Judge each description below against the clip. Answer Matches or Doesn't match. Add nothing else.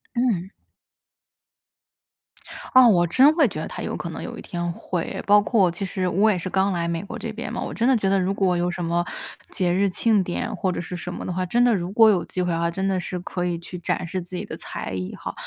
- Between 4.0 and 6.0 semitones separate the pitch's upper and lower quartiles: Doesn't match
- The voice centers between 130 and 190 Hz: Matches